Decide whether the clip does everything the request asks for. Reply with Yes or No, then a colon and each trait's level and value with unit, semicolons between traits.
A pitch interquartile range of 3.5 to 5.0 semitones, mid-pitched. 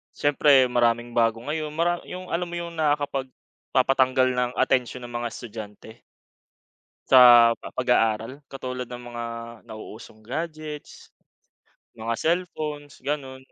No: average, 4.0 semitones; low, 130 Hz